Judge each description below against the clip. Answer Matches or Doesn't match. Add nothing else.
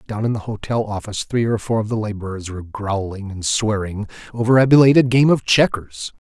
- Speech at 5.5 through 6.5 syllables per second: Matches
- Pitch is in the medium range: Doesn't match